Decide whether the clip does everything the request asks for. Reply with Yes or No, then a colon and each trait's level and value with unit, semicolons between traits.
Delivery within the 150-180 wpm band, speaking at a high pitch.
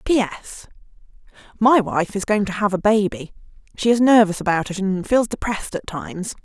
Yes: average, 175 wpm; high, 200 Hz